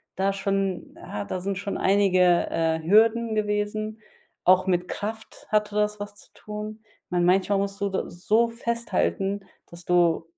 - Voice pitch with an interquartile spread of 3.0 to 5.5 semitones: No, narrow, 2.6 semitones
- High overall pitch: Yes, high, 200 Hz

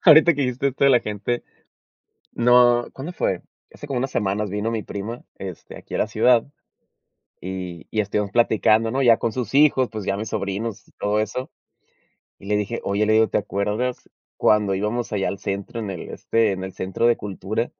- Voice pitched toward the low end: Yes, low, 110 Hz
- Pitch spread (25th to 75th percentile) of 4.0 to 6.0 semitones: No, average, 3.3 semitones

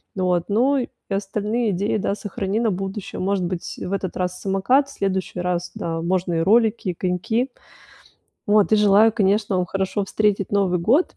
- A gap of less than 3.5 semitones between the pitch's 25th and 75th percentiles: Yes, average, 2.8 semitones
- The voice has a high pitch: Yes, high, 195 Hz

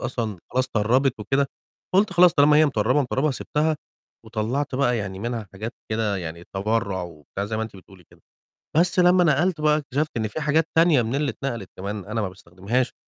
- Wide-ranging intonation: Yes, wide, 6.2 semitones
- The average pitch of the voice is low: Yes, low, 120 Hz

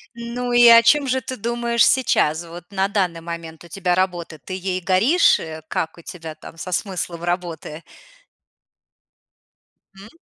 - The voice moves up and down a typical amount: No, wide, 5.8 semitones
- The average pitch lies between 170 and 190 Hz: Yes, medium, 185 Hz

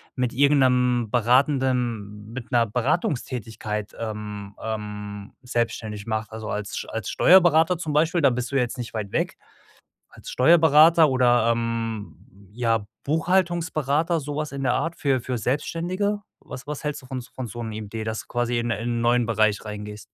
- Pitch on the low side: Yes, low, 120 Hz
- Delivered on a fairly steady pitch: No, average, 4.7 semitones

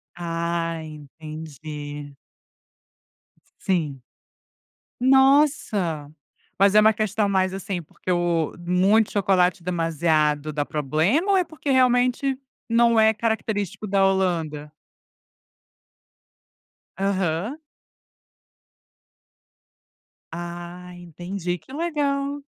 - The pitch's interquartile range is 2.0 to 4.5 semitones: No, average, 5.2 semitones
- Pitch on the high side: No, medium, 180 Hz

